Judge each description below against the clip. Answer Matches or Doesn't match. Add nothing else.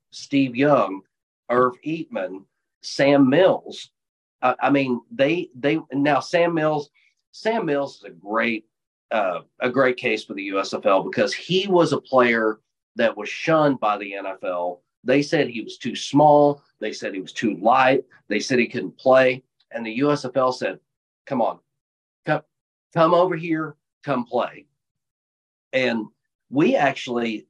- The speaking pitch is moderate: Doesn't match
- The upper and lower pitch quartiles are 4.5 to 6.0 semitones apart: Matches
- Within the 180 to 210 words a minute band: Doesn't match